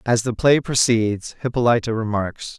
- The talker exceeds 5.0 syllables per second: No, 4.6 syllables/s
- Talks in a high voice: No, low, 115 Hz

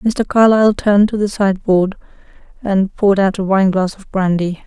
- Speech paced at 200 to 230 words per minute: No, average, 165 wpm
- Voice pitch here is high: Yes, high, 195 Hz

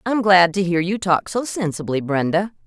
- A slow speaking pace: No, average, 200 wpm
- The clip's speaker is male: No, female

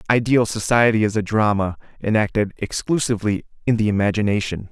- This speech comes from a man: Yes, male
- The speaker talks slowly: Yes, slow, 125 wpm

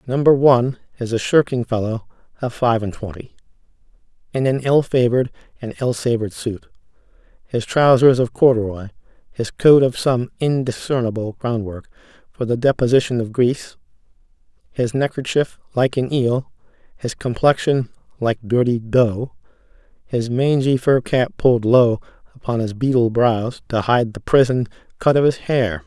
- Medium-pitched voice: No, low, 125 Hz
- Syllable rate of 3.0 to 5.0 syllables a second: Yes, 4.8 syllables/s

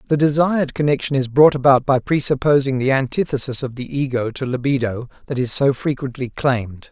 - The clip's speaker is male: Yes, male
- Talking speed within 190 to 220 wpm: No, average, 175 wpm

